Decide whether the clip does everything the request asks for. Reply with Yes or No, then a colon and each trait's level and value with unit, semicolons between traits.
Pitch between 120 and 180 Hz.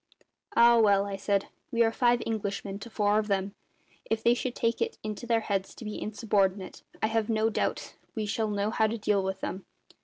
No: high, 215 Hz